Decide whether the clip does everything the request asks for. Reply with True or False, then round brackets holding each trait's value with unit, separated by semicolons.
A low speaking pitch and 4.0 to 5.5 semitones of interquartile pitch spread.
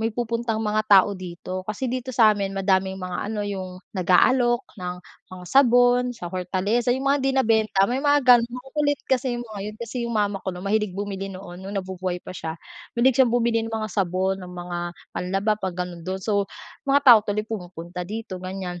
False (205 Hz; 4.3 semitones)